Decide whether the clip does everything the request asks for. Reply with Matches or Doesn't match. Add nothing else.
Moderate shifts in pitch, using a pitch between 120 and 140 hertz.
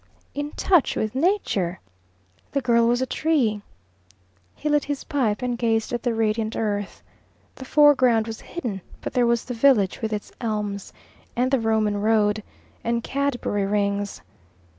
Doesn't match